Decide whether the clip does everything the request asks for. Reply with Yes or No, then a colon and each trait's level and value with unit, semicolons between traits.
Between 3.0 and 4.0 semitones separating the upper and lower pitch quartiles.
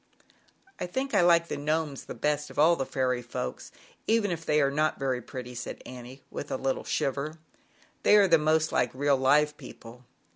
Yes: average, 3.6 semitones